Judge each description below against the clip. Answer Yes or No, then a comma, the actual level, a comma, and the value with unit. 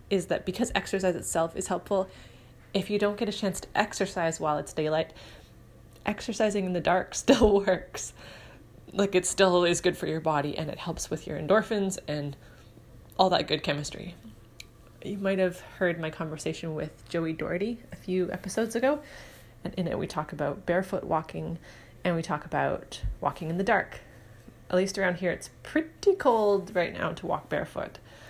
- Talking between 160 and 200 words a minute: Yes, average, 180 wpm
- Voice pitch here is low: No, medium, 175 Hz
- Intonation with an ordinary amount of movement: Yes, average, 4.3 semitones